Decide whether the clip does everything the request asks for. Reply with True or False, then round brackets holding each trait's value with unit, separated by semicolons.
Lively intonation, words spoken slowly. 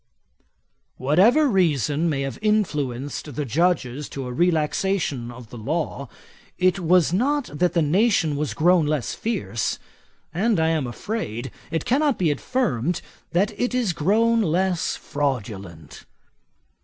True (6.0 semitones; 130 wpm)